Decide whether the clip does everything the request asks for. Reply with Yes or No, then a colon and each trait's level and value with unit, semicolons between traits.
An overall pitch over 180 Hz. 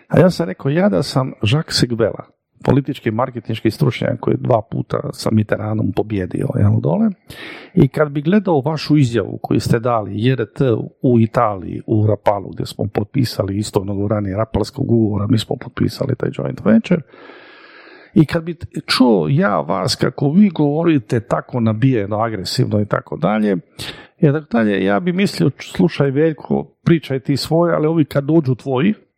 No: low, 135 Hz